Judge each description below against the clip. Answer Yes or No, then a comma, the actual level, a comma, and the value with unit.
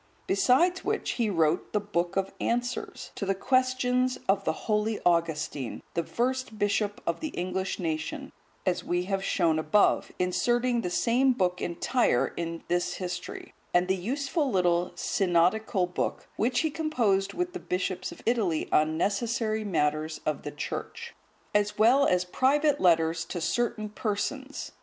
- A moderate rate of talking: Yes, average, 150 wpm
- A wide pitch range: Yes, wide, 5.7 semitones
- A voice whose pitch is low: No, high, 200 Hz